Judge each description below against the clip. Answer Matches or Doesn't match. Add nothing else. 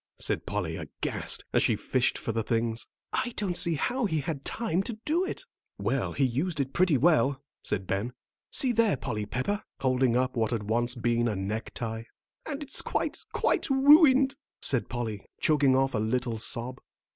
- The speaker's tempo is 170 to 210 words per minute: Matches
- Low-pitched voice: Matches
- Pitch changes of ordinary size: Doesn't match